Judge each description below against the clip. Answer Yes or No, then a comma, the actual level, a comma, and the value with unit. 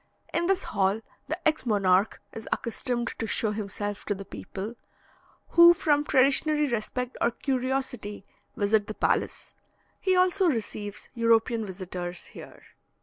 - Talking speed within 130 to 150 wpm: Yes, slow, 135 wpm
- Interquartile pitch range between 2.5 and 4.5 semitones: No, average, 5.0 semitones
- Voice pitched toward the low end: No, high, 230 Hz